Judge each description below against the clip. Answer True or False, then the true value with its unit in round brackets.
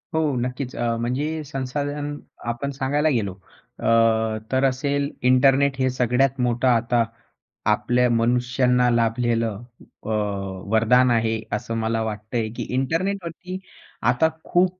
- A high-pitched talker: False (125 Hz)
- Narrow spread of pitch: False (3.3 semitones)